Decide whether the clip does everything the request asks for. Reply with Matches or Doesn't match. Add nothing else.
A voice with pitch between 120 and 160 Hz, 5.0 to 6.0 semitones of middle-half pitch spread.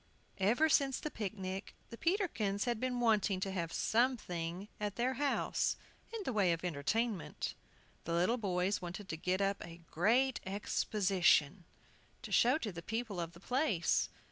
Doesn't match